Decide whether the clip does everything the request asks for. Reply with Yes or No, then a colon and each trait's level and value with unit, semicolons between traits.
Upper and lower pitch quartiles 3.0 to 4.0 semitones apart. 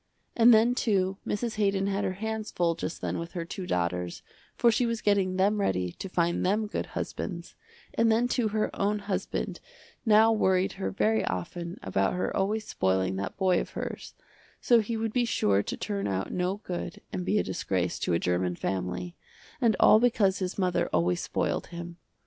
No: average, 4.4 semitones